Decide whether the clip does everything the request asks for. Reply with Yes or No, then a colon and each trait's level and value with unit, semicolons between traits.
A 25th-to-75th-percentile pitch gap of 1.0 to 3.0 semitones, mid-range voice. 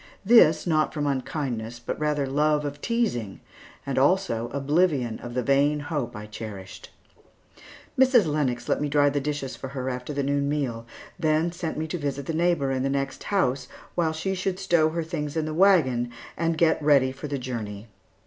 No: average, 3.5 semitones; medium, 145 Hz